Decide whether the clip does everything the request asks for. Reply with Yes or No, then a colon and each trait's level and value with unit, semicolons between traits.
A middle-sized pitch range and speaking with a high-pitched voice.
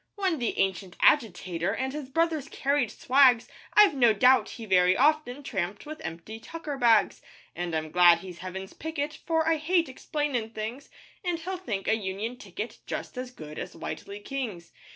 No: wide, 7.5 semitones; high, 245 Hz